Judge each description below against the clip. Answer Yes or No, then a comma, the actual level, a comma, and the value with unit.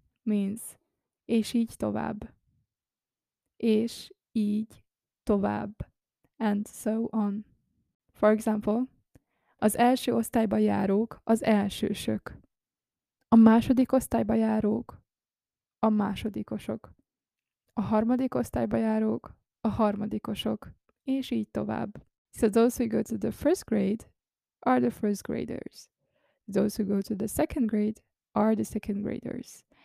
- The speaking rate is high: No, average, 115 wpm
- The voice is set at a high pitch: Yes, high, 220 Hz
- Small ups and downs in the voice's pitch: Yes, narrow, 2.0 semitones